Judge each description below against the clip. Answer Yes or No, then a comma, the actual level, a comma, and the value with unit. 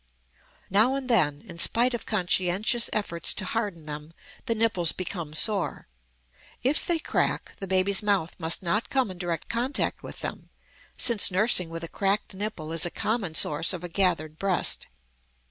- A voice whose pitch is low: No, high, 190 Hz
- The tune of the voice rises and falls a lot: No, average, 4.5 semitones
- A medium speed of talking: Yes, average, 165 wpm